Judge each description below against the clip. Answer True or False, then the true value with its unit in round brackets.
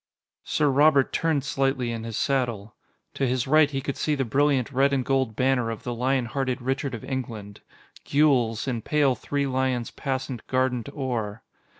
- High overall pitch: False (130 Hz)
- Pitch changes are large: False (2.4 semitones)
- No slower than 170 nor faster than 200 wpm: True (175 wpm)